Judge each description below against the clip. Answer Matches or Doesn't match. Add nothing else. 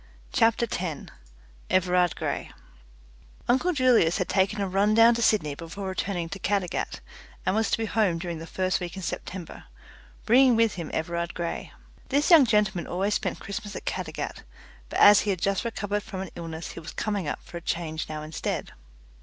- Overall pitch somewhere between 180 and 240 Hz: Matches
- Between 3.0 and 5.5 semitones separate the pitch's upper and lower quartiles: Matches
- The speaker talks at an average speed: Matches